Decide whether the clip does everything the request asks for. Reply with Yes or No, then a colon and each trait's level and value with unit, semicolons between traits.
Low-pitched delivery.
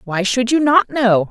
No: high, 235 Hz